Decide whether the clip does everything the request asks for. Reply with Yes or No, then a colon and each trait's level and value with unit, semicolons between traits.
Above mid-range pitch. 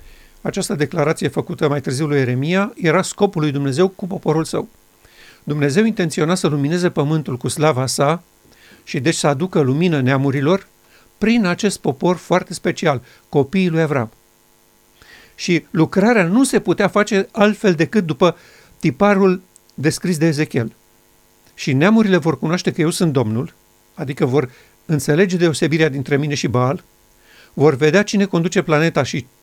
No: medium, 160 Hz